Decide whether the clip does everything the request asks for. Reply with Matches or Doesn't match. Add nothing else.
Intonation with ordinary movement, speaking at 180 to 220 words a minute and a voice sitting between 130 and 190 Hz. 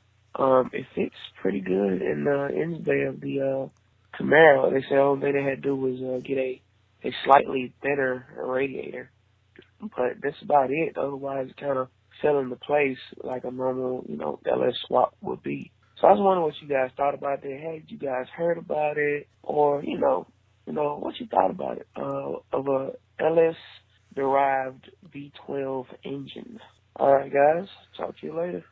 Doesn't match